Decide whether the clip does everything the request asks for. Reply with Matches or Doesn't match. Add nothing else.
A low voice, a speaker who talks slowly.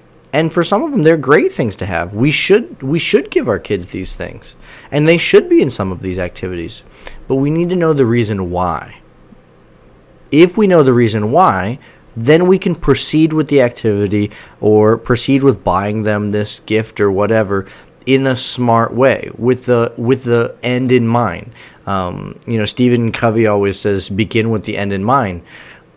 Doesn't match